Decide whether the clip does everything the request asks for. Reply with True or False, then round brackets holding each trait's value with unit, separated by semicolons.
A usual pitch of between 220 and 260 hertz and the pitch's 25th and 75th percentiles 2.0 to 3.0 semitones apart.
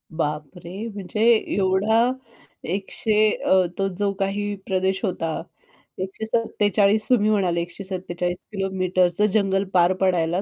False (190 Hz; 2.4 semitones)